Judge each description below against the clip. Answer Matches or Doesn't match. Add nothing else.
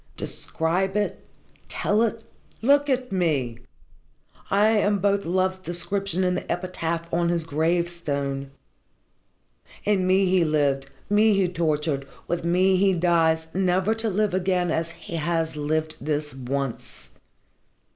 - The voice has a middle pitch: Matches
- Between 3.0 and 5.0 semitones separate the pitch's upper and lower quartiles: Matches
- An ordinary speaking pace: Doesn't match